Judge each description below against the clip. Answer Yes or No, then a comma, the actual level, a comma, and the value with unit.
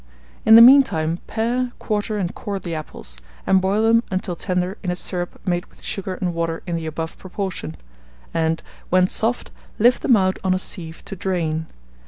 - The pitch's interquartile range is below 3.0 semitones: No, average, 3.7 semitones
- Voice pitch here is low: No, medium, 185 Hz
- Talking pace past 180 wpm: Yes, average, 190 wpm